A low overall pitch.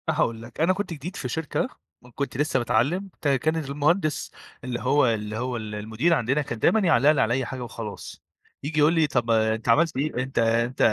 Yes: low, 130 Hz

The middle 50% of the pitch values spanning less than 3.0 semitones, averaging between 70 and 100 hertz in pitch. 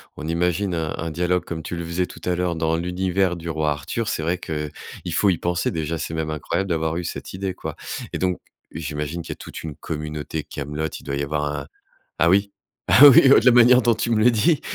No: average, 3.3 semitones; very low, 85 Hz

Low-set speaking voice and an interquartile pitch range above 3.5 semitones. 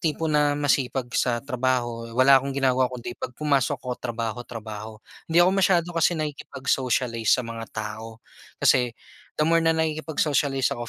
Yes: low, 130 Hz; average, 4.2 semitones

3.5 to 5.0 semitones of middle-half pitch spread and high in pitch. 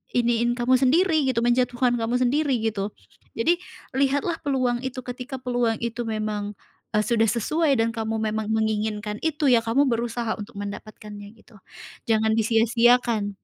No: average, 2.7 semitones; high, 235 Hz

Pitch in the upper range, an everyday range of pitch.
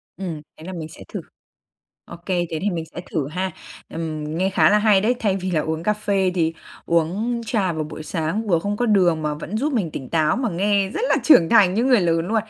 No: medium, 180 Hz; average, 4.3 semitones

